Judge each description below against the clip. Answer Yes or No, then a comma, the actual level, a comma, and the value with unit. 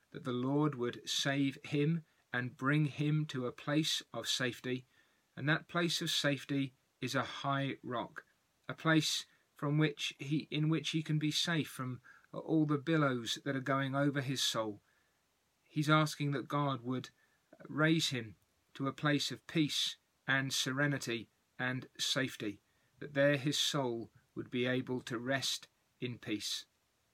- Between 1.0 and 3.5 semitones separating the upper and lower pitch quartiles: Yes, average, 3.0 semitones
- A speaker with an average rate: Yes, average, 155 wpm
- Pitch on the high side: No, medium, 140 Hz